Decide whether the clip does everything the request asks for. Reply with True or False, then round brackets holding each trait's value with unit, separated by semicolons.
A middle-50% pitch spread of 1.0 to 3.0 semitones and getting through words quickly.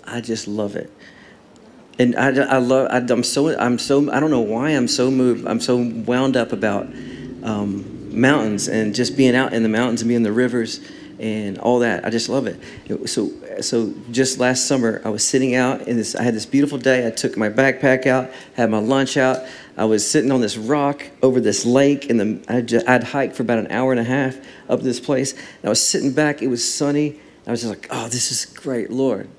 True (2.5 semitones; 225 wpm)